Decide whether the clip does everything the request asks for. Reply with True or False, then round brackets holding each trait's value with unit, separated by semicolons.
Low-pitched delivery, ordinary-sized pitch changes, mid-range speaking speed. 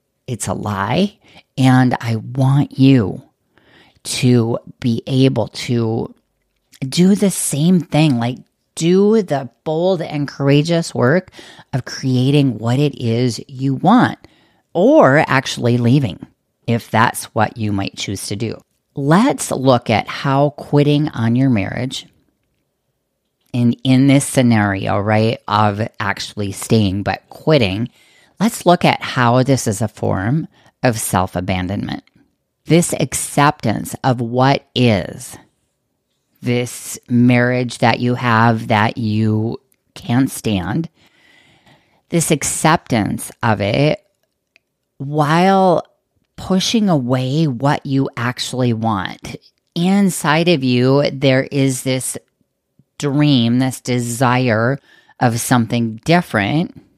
False (130 Hz; 3.9 semitones; 110 wpm)